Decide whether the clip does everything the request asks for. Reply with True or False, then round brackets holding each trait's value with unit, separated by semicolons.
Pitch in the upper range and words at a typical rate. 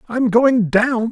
False (235 Hz; 215 wpm)